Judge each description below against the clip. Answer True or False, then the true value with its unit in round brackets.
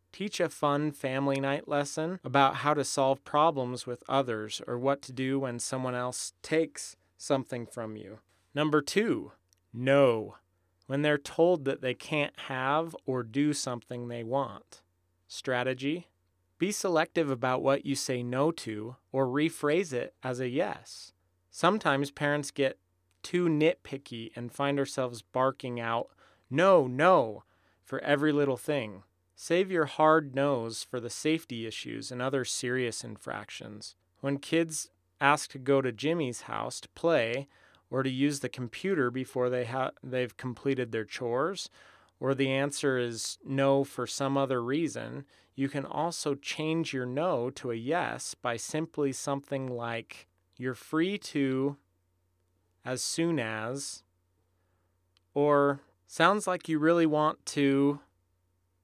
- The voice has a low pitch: True (130 Hz)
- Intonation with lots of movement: False (4.1 semitones)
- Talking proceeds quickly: False (140 wpm)